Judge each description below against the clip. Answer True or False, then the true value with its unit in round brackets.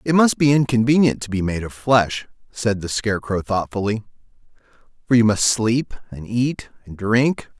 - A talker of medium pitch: False (115 Hz)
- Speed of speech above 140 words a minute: True (165 wpm)